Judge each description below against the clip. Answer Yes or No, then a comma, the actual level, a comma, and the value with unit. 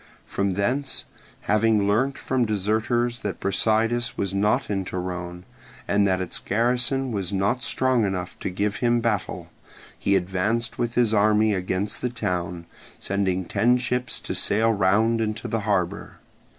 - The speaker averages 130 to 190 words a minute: Yes, average, 150 wpm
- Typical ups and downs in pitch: Yes, average, 3.6 semitones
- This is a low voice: Yes, low, 105 Hz